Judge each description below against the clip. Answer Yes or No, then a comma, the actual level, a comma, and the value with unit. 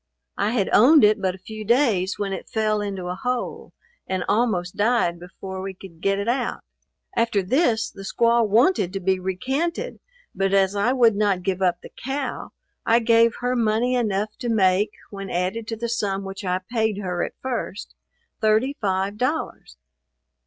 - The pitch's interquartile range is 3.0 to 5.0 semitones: Yes, average, 3.6 semitones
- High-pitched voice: Yes, high, 210 Hz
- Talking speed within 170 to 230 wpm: Yes, average, 180 wpm